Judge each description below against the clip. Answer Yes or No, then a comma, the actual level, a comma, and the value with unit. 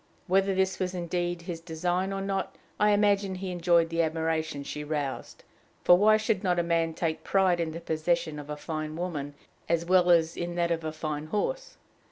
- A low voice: No, medium, 170 Hz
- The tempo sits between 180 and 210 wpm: Yes, average, 200 wpm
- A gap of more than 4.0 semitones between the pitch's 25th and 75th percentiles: No, narrow, 2.6 semitones